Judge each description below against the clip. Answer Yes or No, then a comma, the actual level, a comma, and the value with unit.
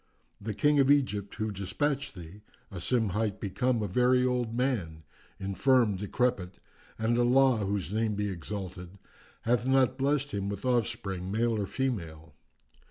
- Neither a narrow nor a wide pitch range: Yes, average, 4.5 semitones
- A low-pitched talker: Yes, low, 110 Hz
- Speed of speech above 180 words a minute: No, average, 150 wpm